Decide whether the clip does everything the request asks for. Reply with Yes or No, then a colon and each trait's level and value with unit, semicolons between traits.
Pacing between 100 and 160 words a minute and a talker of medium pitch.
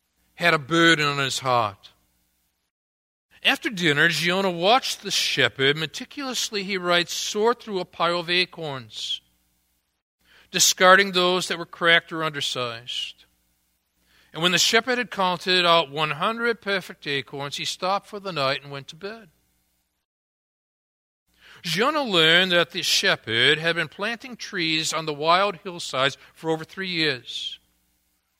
Yes: slow, 135 wpm; medium, 160 Hz